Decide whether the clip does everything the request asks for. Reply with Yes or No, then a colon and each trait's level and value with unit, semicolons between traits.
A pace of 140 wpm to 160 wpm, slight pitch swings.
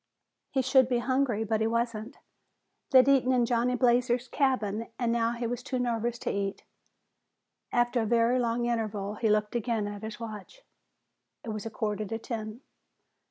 No: average, 170 wpm; narrow, 2.2 semitones